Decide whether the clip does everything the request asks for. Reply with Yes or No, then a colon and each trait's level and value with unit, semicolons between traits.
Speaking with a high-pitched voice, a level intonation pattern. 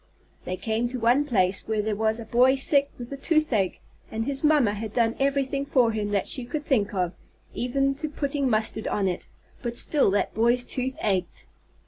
No: high, 240 Hz; average, 4.2 semitones